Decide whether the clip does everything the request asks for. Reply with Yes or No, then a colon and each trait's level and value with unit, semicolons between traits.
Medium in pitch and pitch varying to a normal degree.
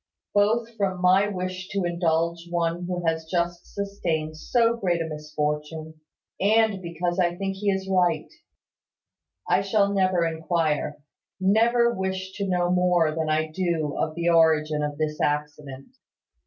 Yes: medium, 175 Hz; average, 3.3 semitones